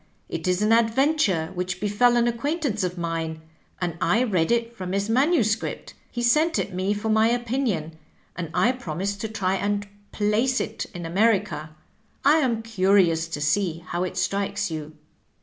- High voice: Yes, high, 205 Hz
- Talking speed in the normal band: Yes, average, 170 wpm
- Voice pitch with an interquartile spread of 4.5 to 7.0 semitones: Yes, average, 4.9 semitones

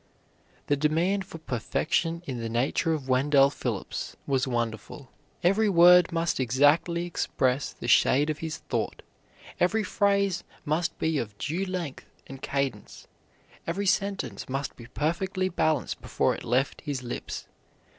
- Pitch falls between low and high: Yes, medium, 155 Hz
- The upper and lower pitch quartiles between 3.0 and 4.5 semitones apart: No, average, 5.1 semitones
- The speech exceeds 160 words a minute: No, average, 140 wpm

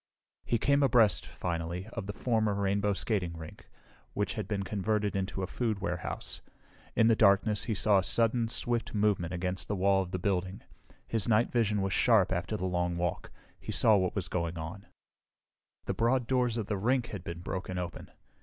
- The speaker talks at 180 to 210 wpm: Yes, average, 190 wpm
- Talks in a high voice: No, low, 100 Hz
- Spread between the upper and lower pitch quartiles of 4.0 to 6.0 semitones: No, average, 3.3 semitones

